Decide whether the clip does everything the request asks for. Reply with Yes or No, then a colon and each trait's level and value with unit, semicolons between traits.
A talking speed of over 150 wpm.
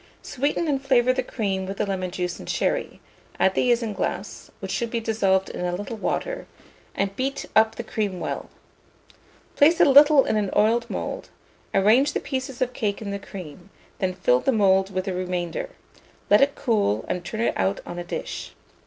Yes: average, 190 wpm